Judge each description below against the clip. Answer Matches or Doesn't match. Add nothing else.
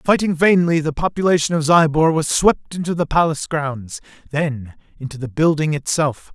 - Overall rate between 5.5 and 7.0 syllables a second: Doesn't match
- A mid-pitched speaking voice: Matches